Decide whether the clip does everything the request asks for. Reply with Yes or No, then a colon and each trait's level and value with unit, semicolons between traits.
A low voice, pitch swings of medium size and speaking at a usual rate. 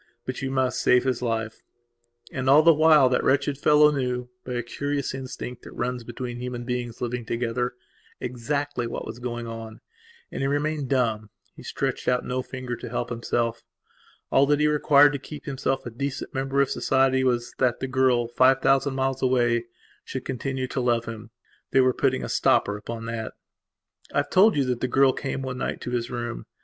No: low, 125 Hz; narrow, 2.1 semitones; average, 190 wpm